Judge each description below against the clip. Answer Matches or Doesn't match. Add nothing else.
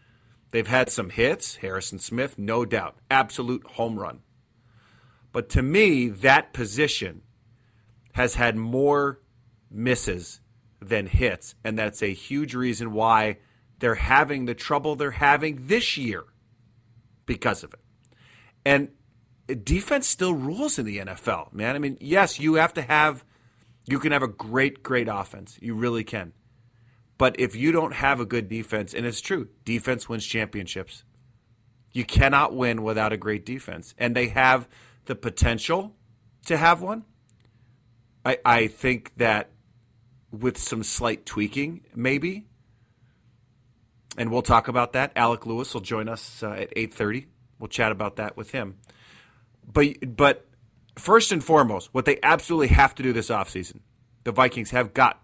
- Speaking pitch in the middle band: Doesn't match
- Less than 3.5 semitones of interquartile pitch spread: Matches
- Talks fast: Doesn't match